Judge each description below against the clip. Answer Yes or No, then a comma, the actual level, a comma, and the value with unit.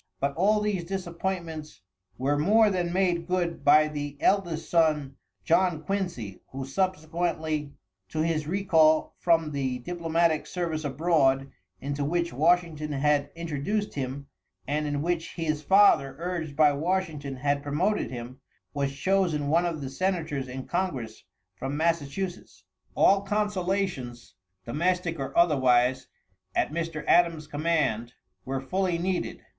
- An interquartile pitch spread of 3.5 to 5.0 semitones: Yes, average, 3.8 semitones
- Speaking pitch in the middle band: Yes, medium, 160 Hz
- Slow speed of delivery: Yes, slow, 130 wpm